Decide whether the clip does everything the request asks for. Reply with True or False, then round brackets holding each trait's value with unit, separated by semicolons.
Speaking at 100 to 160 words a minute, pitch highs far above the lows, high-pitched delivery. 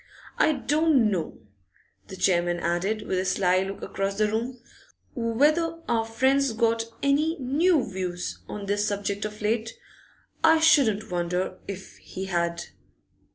True (140 wpm; 5.7 semitones; 215 Hz)